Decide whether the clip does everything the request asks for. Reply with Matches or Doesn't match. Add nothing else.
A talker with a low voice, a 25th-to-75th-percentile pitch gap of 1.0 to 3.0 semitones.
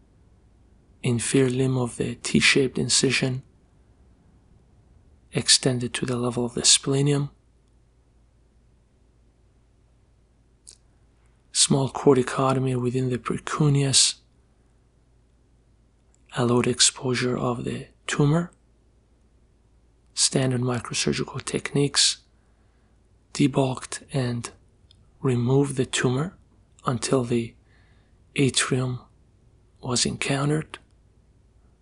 Matches